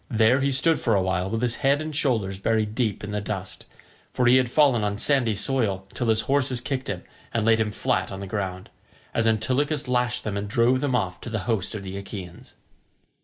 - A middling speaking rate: No, fast, 220 wpm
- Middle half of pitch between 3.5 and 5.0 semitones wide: Yes, average, 4.2 semitones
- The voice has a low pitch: Yes, low, 115 Hz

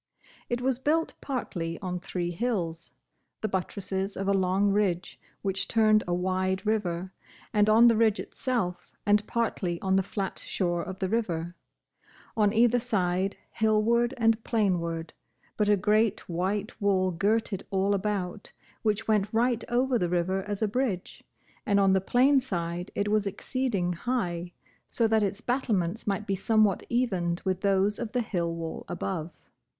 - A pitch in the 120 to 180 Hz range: No, high, 200 Hz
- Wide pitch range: No, average, 3.4 semitones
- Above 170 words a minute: No, average, 160 wpm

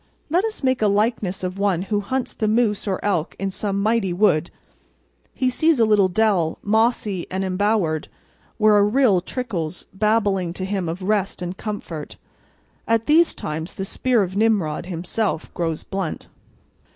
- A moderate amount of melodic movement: Yes, average, 3.4 semitones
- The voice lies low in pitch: No, high, 200 Hz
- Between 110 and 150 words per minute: No, average, 165 wpm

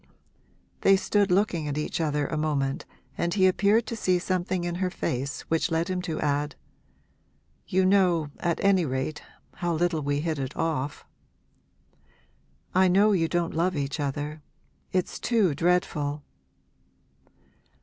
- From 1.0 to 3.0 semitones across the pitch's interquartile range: No, average, 3.8 semitones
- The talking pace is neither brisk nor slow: Yes, average, 145 wpm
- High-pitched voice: No, medium, 170 Hz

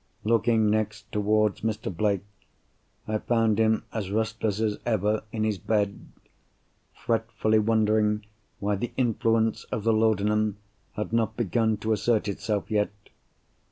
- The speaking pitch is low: Yes, low, 110 Hz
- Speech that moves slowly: Yes, slow, 130 wpm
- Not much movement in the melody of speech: Yes, narrow, 1.2 semitones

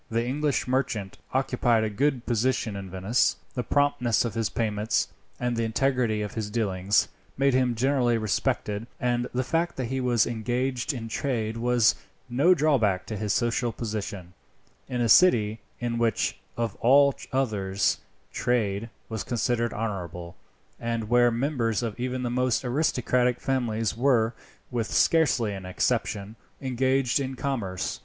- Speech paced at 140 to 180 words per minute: Yes, average, 150 wpm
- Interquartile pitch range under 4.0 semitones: Yes, average, 2.8 semitones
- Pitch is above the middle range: No, low, 120 Hz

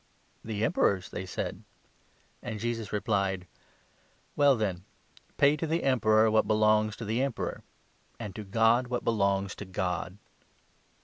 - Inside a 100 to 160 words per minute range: Yes, average, 145 wpm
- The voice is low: Yes, low, 110 Hz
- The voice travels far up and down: No, average, 3.1 semitones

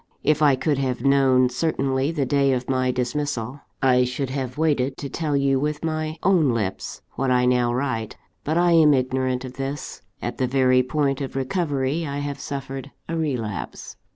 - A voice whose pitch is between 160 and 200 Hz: No, low, 135 Hz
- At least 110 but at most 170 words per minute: No, average, 180 wpm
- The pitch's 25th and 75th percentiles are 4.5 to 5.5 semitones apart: No, narrow, 2.4 semitones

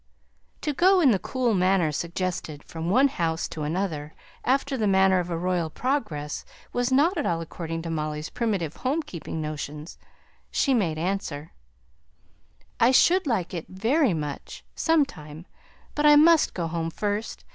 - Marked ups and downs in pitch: Yes, wide, 8.1 semitones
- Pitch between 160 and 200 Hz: Yes, medium, 185 Hz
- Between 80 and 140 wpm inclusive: No, average, 160 wpm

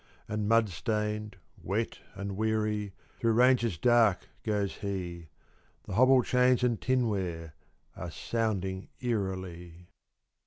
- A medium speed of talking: No, slow, 110 wpm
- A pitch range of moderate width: Yes, average, 3.5 semitones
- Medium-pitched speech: No, low, 105 Hz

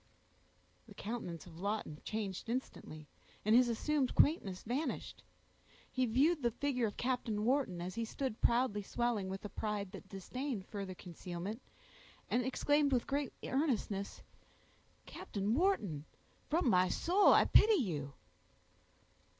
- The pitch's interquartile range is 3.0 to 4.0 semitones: No, average, 5.3 semitones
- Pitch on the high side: Yes, high, 225 Hz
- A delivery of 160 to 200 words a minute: No, slow, 135 wpm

